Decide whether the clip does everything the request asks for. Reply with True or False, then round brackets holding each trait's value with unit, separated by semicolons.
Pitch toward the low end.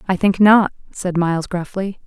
False (190 Hz)